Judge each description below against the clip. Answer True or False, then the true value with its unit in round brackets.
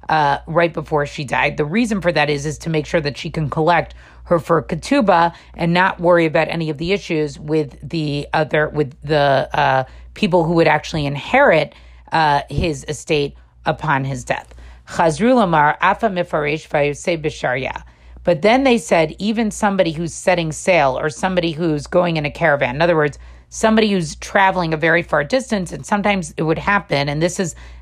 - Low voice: False (160 Hz)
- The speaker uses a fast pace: False (175 wpm)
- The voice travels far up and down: False (3.2 semitones)